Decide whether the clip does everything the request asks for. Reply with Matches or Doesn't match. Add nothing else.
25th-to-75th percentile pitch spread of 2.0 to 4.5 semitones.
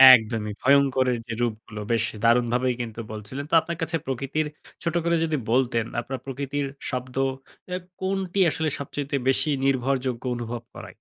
Matches